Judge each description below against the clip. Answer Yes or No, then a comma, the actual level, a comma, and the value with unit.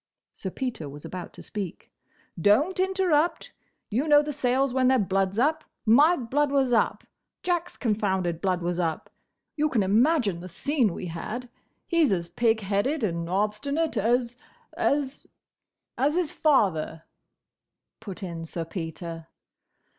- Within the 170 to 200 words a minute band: No, average, 140 wpm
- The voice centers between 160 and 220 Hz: No, high, 230 Hz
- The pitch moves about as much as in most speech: No, wide, 7.9 semitones